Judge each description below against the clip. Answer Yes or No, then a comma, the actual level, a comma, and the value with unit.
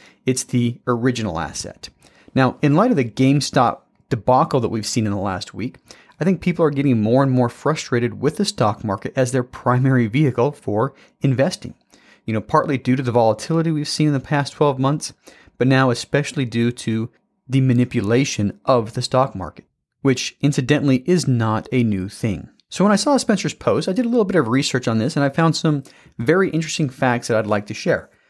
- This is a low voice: Yes, low, 130 Hz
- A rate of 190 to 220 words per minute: Yes, fast, 205 wpm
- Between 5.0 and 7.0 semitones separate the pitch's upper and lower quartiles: No, average, 3.8 semitones